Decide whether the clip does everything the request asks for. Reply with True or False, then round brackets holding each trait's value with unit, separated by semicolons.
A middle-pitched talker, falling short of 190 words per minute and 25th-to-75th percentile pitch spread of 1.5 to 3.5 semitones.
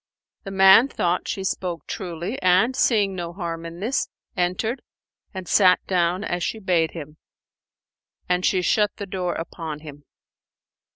True (180 Hz; 150 wpm; 2.4 semitones)